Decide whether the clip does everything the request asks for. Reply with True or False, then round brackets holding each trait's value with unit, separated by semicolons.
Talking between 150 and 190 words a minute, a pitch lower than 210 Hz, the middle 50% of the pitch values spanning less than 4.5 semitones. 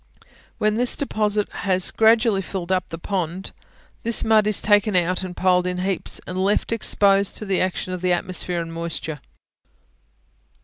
True (165 wpm; 190 Hz; 2.5 semitones)